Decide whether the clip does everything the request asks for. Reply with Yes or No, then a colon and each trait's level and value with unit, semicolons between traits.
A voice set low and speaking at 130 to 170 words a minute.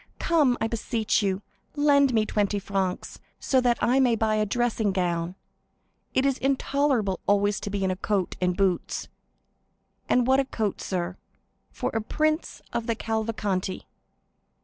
No: high, 220 Hz; average, 155 wpm